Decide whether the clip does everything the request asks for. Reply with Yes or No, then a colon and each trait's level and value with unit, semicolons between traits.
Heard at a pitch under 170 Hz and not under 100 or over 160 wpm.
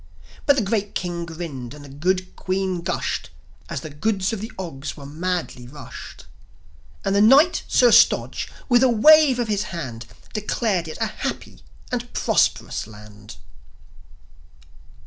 No: medium, 180 Hz; average, 145 wpm